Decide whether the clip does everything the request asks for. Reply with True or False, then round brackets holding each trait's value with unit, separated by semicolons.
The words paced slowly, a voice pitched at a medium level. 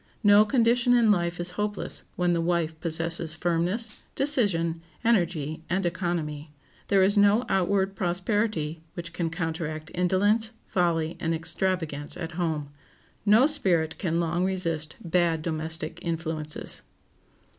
True (125 wpm; 175 Hz)